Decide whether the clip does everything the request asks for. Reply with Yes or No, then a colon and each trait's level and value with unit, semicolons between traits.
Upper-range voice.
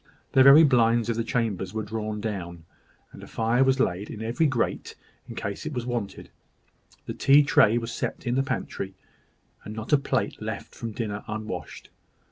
No: low, 115 Hz